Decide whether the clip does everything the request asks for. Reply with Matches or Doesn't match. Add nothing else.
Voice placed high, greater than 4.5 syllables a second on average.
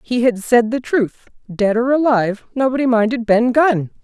Matches